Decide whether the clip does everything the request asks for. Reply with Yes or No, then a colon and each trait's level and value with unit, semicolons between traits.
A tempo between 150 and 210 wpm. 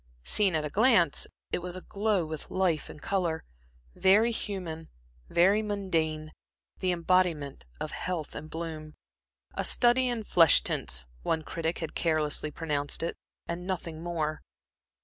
No: average, 140 wpm